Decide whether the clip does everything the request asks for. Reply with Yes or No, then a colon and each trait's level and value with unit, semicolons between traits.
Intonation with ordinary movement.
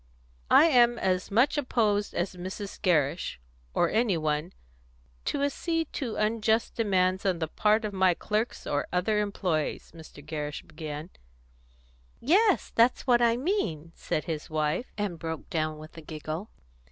No: wide, 6.3 semitones